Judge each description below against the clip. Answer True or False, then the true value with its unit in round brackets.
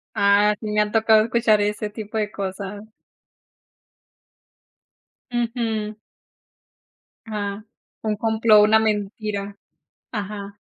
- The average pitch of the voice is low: False (210 Hz)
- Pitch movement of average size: False (1.3 semitones)